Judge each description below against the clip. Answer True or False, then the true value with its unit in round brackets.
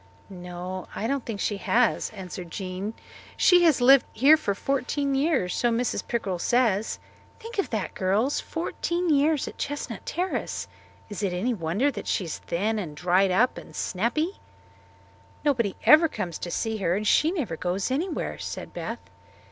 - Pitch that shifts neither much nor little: False (7.0 semitones)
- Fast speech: False (165 wpm)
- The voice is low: False (225 Hz)